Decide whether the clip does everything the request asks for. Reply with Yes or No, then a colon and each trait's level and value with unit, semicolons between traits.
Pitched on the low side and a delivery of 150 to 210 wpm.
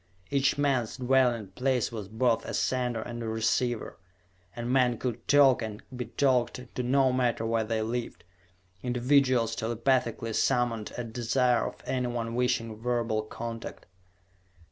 No: low, 120 Hz; average, 140 wpm